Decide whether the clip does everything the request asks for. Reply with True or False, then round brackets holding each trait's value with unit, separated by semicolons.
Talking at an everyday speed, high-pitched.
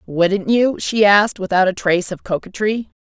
True (180 wpm; 200 Hz)